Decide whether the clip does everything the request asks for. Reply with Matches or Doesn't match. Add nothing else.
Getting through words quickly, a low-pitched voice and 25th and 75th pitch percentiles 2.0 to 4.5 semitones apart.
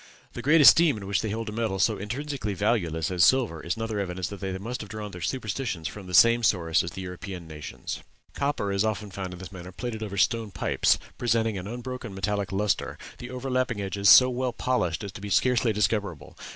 Matches